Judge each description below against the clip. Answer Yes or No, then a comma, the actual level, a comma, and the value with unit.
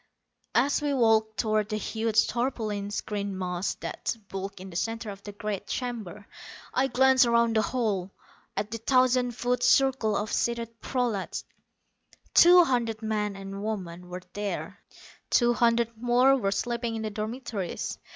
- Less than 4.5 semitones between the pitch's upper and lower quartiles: Yes, average, 3.1 semitones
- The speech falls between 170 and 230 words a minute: No, average, 150 wpm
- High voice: Yes, high, 220 Hz